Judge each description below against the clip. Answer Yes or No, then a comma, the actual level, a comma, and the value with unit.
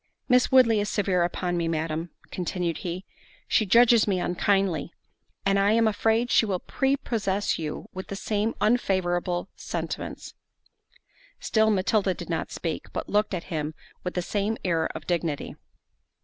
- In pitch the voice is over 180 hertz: Yes, high, 190 Hz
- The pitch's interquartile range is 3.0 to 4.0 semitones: Yes, average, 3.7 semitones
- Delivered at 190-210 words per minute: No, average, 150 wpm